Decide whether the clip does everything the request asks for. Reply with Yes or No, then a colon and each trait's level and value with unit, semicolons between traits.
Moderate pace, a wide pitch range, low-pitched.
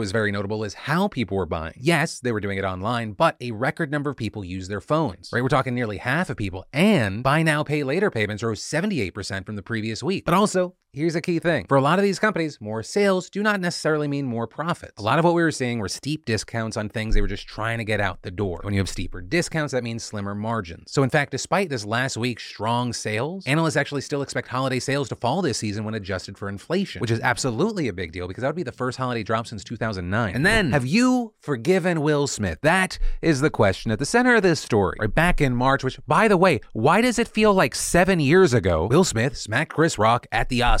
No: fast, 255 wpm; wide, 7.1 semitones; low, 130 Hz